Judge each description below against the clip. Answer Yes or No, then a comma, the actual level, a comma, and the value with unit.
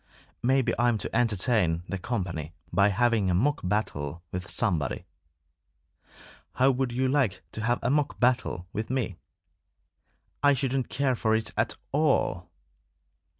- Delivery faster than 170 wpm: No, average, 140 wpm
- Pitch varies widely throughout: Yes, wide, 5.8 semitones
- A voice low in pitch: Yes, low, 115 Hz